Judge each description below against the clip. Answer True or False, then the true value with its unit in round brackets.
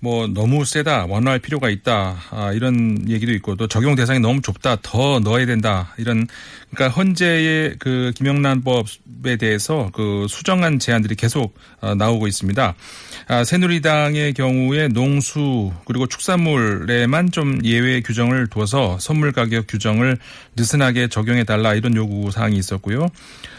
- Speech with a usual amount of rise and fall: True (4.1 semitones)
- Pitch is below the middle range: True (120 Hz)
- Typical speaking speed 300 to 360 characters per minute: True (320 characters per minute)